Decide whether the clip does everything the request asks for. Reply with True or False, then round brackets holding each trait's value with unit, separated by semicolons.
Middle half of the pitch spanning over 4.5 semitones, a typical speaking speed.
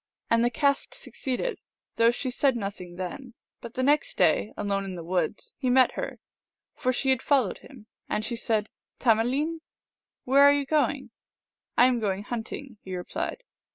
True (4.9 semitones; 190 wpm)